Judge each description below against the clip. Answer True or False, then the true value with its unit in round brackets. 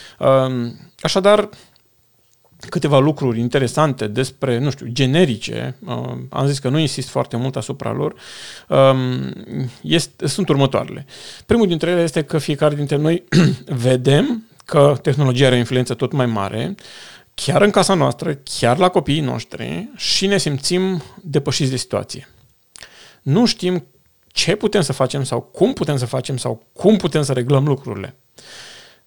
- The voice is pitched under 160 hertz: True (140 Hz)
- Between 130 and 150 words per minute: True (140 wpm)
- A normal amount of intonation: True (4.5 semitones)